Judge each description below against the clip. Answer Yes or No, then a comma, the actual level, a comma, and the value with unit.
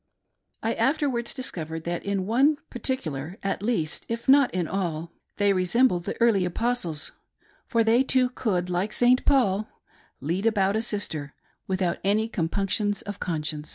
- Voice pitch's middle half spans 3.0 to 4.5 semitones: No, average, 5.3 semitones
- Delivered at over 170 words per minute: No, average, 160 wpm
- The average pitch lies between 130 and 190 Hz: No, high, 200 Hz